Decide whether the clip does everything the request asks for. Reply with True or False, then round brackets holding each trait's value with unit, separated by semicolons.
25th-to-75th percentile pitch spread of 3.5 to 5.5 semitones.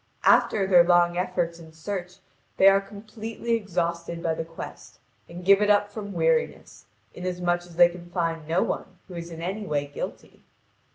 False (2.9 semitones)